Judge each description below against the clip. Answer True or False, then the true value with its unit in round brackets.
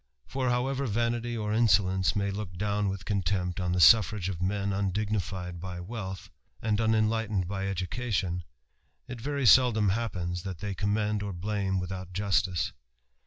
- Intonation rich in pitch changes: False (2.9 semitones)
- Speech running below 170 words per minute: True (150 wpm)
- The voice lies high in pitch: False (100 Hz)